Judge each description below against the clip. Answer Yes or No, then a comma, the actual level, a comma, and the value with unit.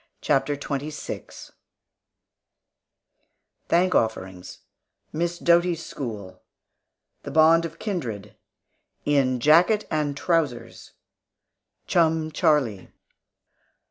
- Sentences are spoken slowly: Yes, slow, 75 wpm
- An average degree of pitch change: Yes, average, 4.6 semitones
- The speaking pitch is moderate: Yes, medium, 150 Hz